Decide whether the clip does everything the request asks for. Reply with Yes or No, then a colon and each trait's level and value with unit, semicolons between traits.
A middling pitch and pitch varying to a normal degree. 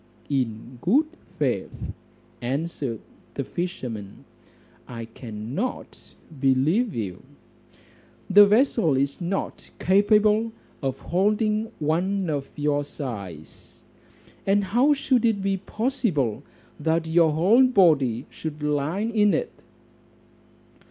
No: medium, 165 Hz; wide, 7.5 semitones